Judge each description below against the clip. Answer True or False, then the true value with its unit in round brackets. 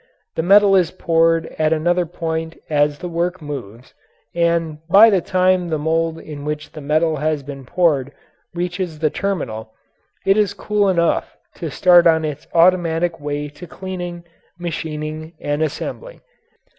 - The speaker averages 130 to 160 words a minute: True (150 wpm)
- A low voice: False (165 Hz)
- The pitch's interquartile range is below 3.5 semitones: True (2.8 semitones)